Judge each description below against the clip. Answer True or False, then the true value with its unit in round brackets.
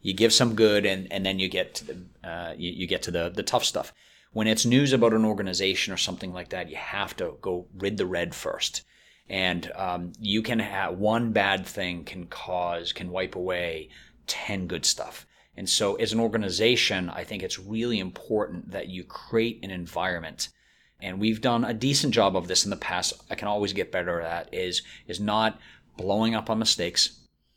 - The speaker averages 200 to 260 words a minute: True (205 wpm)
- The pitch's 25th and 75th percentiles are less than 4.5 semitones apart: True (3.5 semitones)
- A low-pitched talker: True (100 Hz)